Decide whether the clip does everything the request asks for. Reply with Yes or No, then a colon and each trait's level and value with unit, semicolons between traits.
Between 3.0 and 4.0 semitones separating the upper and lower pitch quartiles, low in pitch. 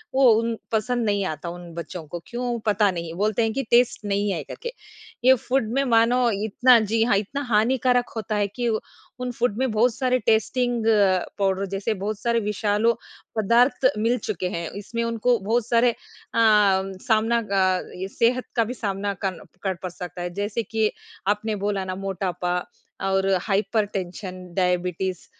No: average, 3.6 semitones; high, 215 Hz